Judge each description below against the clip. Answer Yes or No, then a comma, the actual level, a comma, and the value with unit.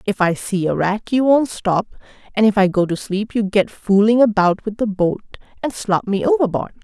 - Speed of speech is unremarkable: No, fast, 220 wpm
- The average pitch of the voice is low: No, high, 210 Hz